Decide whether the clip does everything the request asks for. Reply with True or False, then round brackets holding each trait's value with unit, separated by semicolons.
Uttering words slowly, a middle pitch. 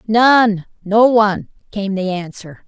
False (110 wpm; 205 Hz)